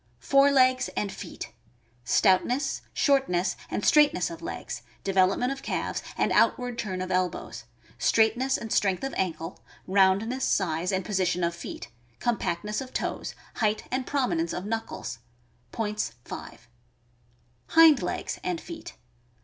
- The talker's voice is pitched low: No, high, 210 Hz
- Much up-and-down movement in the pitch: Yes, wide, 6.1 semitones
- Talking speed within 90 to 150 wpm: Yes, average, 140 wpm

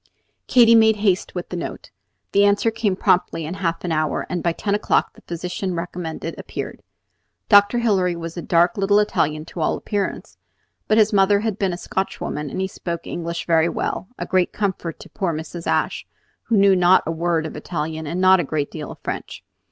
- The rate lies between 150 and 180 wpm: No, fast, 205 wpm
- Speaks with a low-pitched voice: No, medium, 180 Hz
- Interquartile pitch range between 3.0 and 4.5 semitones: Yes, average, 3.3 semitones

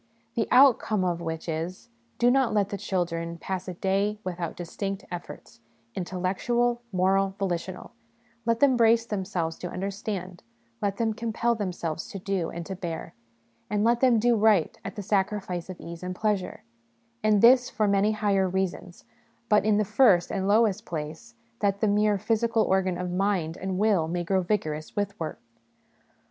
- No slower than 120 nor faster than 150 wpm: No, average, 165 wpm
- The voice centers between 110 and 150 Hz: No, high, 195 Hz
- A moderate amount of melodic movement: Yes, average, 3.2 semitones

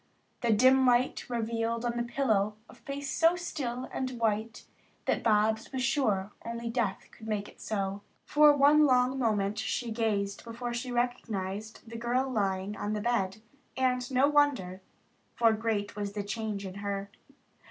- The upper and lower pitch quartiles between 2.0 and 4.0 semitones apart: Yes, average, 3.4 semitones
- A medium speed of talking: Yes, average, 165 wpm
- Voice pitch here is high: Yes, high, 230 Hz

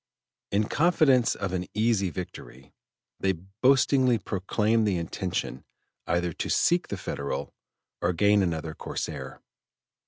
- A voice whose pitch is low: Yes, low, 100 Hz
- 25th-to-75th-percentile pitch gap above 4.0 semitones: Yes, average, 4.7 semitones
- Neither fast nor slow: No, slow, 120 wpm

